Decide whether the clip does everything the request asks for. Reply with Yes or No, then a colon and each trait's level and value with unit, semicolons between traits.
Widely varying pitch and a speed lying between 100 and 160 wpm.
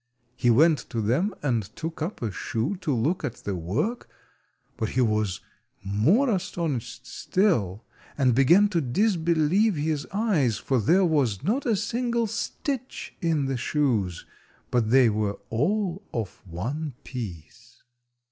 Yes: wide, 8.6 semitones; average, 140 wpm